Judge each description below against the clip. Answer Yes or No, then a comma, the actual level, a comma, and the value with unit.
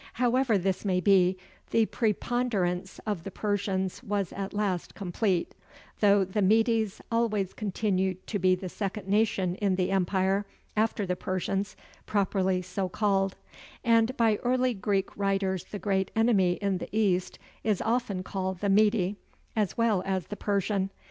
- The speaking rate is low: No, average, 150 wpm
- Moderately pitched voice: No, high, 200 Hz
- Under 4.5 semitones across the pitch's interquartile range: Yes, narrow, 2.4 semitones